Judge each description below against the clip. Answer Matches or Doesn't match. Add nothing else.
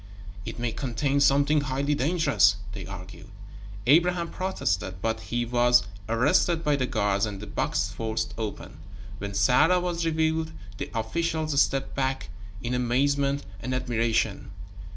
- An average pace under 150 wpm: Matches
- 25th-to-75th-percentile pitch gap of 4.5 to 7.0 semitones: Matches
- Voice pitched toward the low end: Matches